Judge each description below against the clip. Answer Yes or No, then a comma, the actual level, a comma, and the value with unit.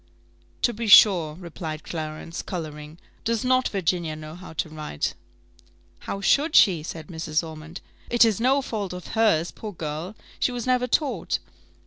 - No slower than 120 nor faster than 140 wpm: No, average, 155 wpm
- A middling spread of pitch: No, wide, 6.3 semitones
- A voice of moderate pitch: Yes, medium, 175 Hz